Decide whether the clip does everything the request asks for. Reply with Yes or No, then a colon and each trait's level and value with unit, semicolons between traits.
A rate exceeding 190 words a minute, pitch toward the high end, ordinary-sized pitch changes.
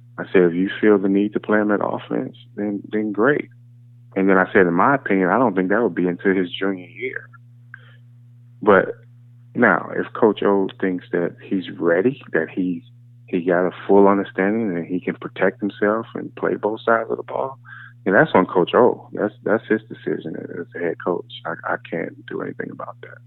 No: fast, 205 wpm; low, 105 Hz; average, 4.0 semitones